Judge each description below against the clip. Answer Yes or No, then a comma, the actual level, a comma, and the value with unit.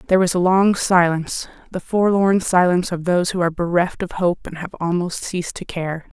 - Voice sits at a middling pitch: Yes, medium, 180 Hz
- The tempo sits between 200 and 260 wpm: Yes, fast, 205 wpm